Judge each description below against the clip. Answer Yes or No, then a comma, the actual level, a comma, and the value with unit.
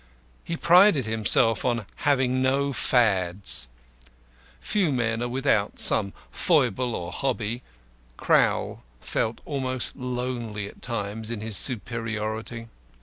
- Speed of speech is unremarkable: No, slow, 110 wpm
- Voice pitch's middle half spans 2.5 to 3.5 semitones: Yes, average, 3.0 semitones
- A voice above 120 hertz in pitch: No, low, 115 Hz